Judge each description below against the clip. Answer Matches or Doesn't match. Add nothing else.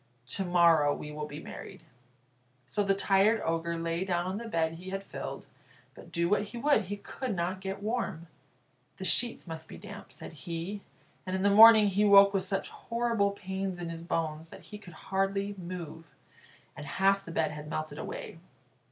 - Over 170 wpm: Matches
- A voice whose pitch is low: Doesn't match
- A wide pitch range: Doesn't match